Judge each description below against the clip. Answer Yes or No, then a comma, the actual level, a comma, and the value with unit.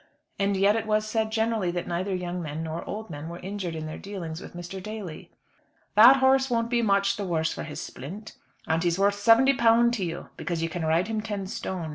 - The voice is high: Yes, high, 195 Hz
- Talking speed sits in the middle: No, fast, 220 wpm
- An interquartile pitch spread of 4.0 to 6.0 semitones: Yes, average, 4.4 semitones